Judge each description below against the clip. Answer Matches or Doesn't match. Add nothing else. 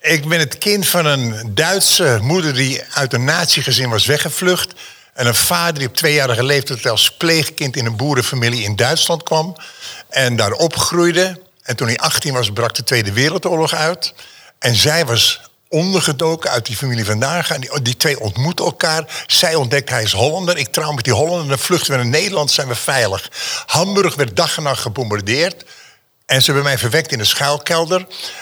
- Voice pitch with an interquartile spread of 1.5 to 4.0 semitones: Doesn't match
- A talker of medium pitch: Matches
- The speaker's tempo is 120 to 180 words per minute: Doesn't match